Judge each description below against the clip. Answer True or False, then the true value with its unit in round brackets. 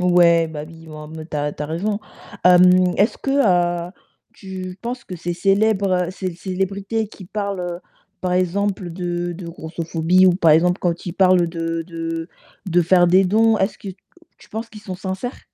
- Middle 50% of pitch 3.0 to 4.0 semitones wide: False (2.5 semitones)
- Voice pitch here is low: False (180 Hz)